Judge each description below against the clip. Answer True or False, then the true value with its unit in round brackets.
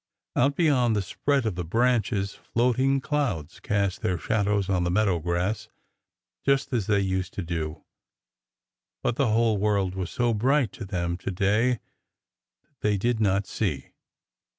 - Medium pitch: False (105 Hz)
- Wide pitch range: False (4.6 semitones)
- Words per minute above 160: False (155 wpm)